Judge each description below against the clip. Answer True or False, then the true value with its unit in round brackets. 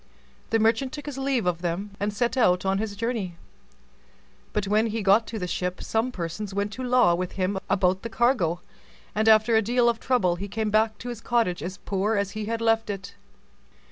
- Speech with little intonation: False (3.2 semitones)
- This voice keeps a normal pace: False (210 wpm)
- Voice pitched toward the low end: False (215 Hz)